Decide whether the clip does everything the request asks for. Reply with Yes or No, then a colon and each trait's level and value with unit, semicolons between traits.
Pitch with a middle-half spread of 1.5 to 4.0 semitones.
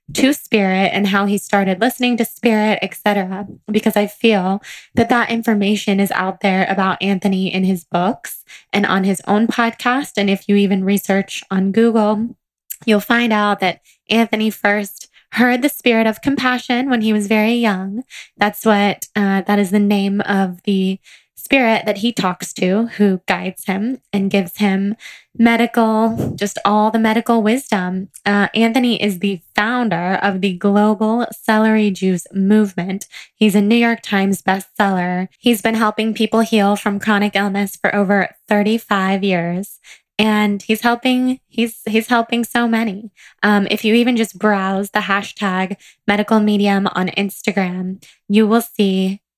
Yes: narrow, 2.4 semitones